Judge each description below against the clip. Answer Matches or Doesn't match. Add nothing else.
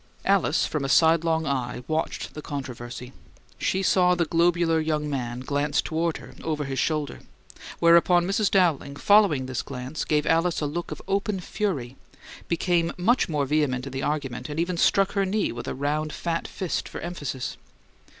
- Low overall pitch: Doesn't match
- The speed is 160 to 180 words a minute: Matches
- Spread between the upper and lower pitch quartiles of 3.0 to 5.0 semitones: Matches